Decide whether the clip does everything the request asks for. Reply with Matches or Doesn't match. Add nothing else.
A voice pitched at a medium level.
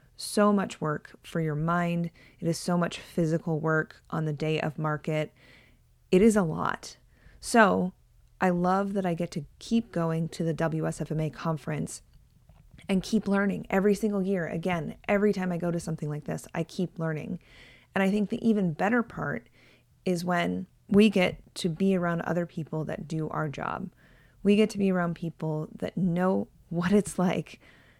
Matches